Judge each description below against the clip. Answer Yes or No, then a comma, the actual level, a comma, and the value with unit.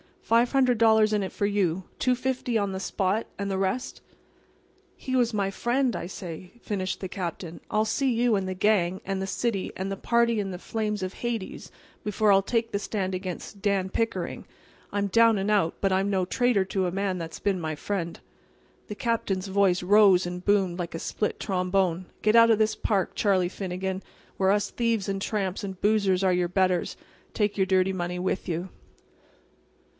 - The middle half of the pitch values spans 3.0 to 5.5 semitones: No, narrow, 2.5 semitones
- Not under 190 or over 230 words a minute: Yes, average, 195 wpm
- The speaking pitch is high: Yes, high, 195 Hz